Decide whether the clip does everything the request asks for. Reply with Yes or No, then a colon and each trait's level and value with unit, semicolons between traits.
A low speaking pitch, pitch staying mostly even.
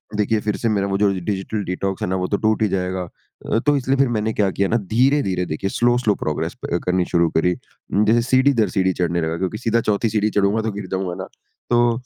No: low, 100 Hz; average, 3.3 semitones